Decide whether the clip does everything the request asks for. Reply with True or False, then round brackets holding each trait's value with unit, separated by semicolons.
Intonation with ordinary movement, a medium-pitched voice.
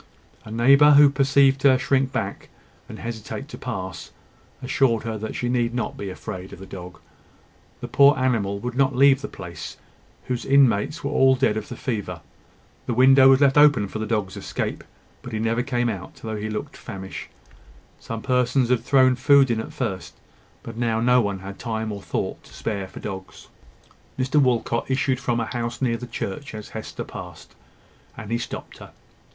False (3.7 semitones; 120 Hz)